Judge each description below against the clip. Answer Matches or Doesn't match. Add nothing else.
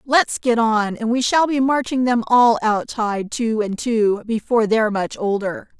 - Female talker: Matches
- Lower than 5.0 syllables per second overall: Matches